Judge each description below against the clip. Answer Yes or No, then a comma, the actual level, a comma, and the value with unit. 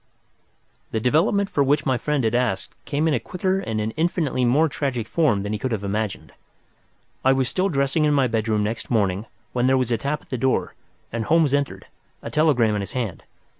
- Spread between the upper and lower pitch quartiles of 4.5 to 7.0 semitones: Yes, average, 5.1 semitones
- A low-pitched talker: Yes, low, 130 Hz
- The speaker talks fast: Yes, fast, 210 wpm